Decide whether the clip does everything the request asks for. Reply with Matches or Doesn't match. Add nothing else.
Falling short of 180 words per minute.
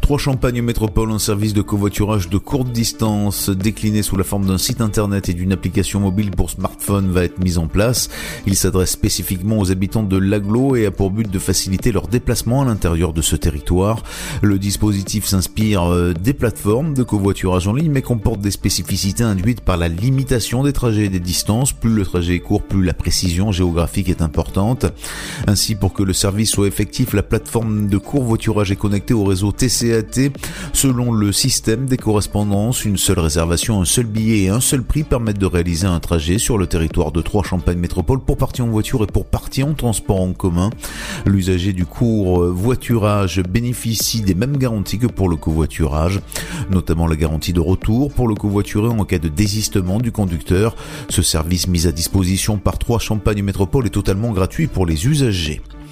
Doesn't match